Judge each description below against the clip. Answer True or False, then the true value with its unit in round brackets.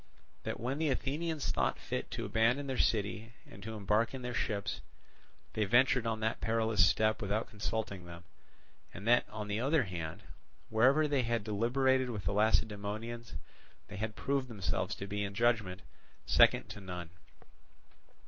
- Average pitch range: True (3.2 semitones)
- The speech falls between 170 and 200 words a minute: False (160 wpm)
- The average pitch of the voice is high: False (110 Hz)